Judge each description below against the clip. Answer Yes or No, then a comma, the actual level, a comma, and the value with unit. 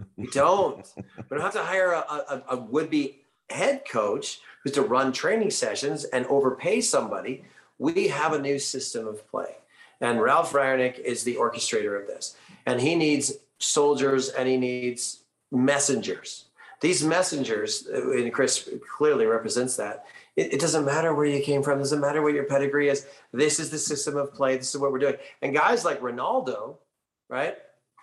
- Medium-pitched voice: Yes, medium, 145 Hz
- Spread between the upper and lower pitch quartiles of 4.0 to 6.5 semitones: Yes, average, 5.0 semitones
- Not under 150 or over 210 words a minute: Yes, average, 180 wpm